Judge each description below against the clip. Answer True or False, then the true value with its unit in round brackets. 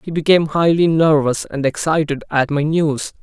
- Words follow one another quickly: False (170 wpm)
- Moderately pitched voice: True (155 Hz)